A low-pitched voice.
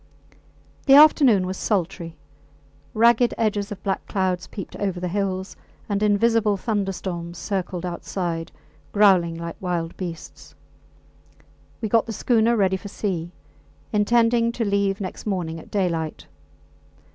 No: high, 195 Hz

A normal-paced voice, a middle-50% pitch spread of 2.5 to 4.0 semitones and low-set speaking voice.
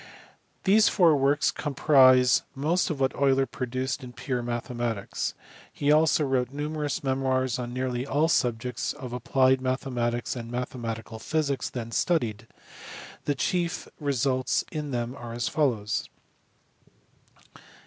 No: slow, 130 wpm; average, 3.0 semitones; low, 130 Hz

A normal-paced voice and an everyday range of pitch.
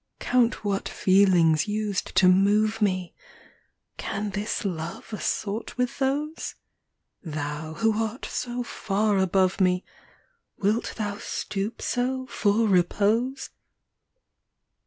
No: slow, 110 wpm; average, 3.3 semitones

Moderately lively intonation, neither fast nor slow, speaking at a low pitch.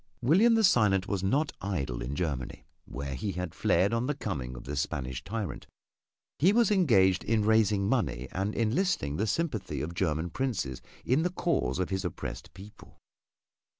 No: wide, 8.5 semitones; average, 170 wpm; low, 100 Hz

